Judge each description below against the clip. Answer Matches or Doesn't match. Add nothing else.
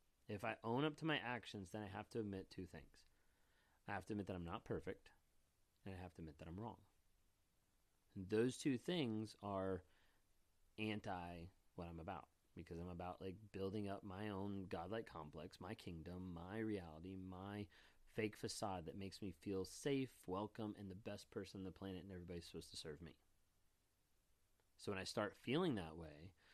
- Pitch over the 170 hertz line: Doesn't match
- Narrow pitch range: Doesn't match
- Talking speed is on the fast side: Doesn't match